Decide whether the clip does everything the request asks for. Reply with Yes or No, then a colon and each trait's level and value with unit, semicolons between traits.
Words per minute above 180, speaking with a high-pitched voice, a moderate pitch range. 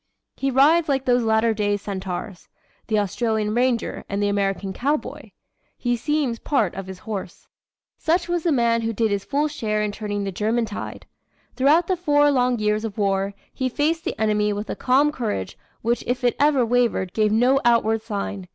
Yes: average, 190 wpm; high, 225 Hz; average, 4.5 semitones